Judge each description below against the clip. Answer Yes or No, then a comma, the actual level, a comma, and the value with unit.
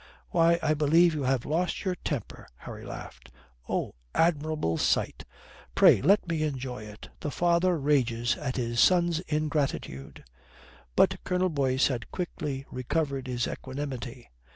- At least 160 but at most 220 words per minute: No, slow, 135 wpm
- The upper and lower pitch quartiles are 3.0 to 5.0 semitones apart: Yes, average, 4.5 semitones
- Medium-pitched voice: Yes, medium, 145 Hz